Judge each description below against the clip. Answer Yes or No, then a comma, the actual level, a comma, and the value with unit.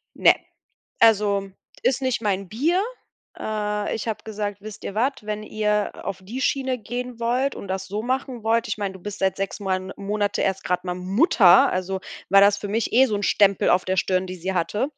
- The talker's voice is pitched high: Yes, high, 205 Hz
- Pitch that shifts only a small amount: No, average, 3.0 semitones